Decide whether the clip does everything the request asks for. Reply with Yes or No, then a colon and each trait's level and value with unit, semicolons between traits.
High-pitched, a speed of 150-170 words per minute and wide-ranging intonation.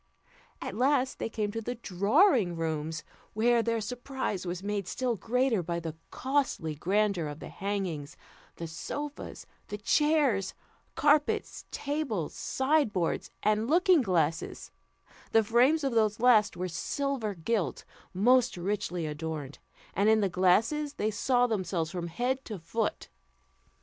No: high, 210 Hz; slow, 135 wpm; wide, 6.2 semitones